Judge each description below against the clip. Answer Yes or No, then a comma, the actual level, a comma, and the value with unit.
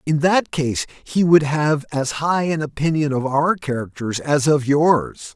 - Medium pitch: Yes, medium, 145 Hz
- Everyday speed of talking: Yes, average, 180 wpm